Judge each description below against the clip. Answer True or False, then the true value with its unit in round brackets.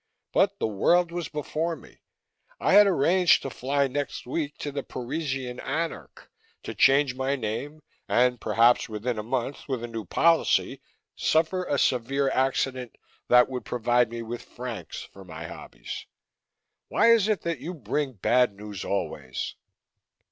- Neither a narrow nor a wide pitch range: True (4.2 semitones)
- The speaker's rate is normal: True (155 wpm)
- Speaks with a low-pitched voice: True (130 Hz)